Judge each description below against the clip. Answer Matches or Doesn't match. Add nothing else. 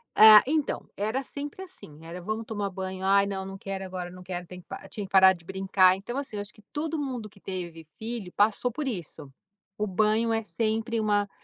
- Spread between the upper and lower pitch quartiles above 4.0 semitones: Doesn't match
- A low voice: Doesn't match